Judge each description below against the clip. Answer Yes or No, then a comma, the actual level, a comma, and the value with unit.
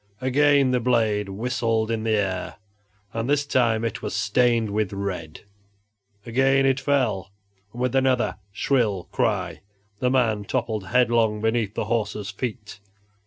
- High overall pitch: No, low, 115 Hz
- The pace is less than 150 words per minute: Yes, average, 140 wpm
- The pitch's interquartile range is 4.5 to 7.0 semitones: No, average, 3.2 semitones